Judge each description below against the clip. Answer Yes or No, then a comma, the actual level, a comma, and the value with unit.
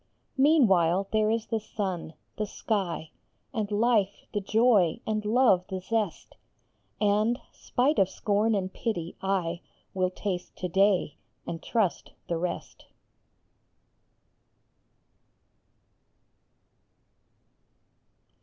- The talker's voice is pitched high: Yes, high, 200 Hz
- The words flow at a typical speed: No, slow, 100 wpm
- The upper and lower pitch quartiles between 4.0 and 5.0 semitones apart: No, average, 3.2 semitones